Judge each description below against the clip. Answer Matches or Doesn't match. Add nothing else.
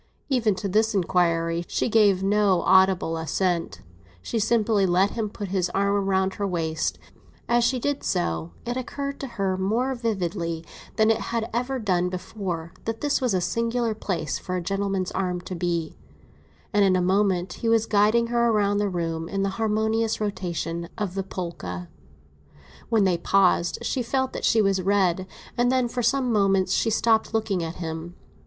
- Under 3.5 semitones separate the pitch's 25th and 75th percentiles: Doesn't match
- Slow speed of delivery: Doesn't match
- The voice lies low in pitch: Doesn't match